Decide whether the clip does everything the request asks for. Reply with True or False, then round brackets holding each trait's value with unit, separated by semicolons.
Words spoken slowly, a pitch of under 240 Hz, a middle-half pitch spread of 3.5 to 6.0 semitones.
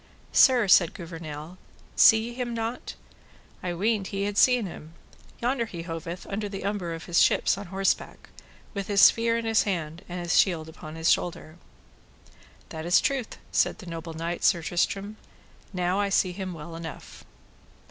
False (170 wpm; 185 Hz; 3.9 semitones)